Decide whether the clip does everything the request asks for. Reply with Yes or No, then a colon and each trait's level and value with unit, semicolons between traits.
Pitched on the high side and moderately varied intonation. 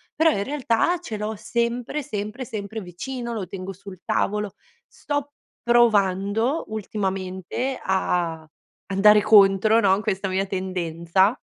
Yes: high, 205 Hz; average, 3.7 semitones